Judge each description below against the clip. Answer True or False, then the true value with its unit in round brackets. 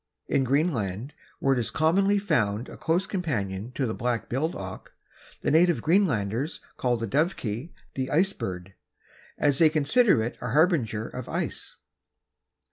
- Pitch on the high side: False (135 Hz)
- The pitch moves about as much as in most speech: False (6.5 semitones)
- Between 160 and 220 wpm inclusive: False (150 wpm)